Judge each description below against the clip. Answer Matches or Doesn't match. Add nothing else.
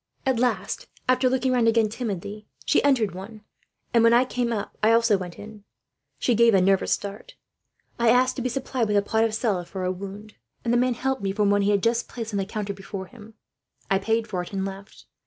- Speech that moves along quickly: Matches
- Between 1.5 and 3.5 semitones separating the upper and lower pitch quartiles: Matches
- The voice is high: Matches